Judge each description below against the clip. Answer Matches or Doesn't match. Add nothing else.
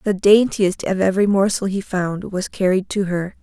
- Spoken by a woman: Matches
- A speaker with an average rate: Matches